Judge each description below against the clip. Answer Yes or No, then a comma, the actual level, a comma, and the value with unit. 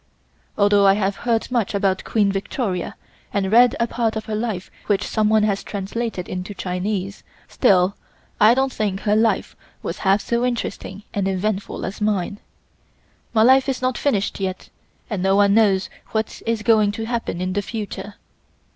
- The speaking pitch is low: No, high, 205 Hz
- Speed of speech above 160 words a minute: Yes, average, 170 wpm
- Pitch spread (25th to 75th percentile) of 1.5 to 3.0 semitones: Yes, narrow, 2.6 semitones